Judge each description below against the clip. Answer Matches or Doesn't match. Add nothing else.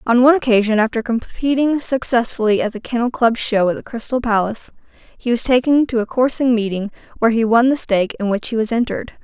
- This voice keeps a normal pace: Doesn't match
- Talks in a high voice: Matches